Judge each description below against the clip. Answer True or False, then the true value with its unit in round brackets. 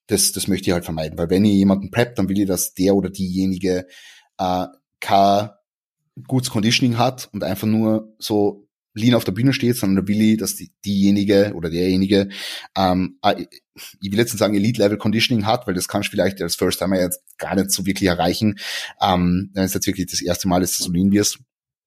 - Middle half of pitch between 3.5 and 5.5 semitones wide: False (2.8 semitones)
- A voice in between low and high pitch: False (100 Hz)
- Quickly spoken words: True (210 wpm)